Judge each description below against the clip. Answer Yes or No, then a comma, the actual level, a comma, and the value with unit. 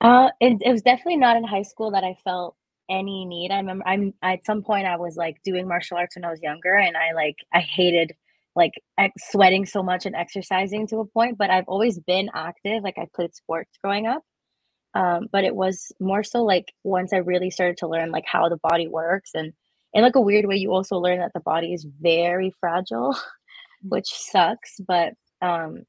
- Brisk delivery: Yes, fast, 215 wpm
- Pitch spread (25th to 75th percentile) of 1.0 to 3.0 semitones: Yes, average, 2.7 semitones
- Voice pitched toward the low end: No, medium, 185 Hz